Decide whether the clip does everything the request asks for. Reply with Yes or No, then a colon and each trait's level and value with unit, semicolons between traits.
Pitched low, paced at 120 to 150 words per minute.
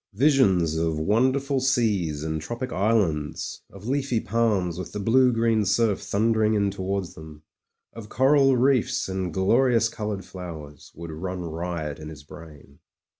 Yes: low, 100 Hz; average, 145 wpm